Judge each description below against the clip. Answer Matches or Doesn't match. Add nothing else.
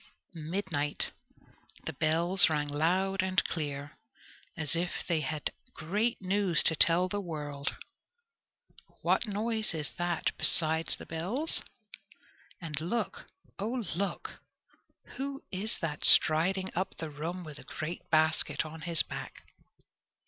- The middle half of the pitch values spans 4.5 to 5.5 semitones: Doesn't match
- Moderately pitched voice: Matches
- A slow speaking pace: Matches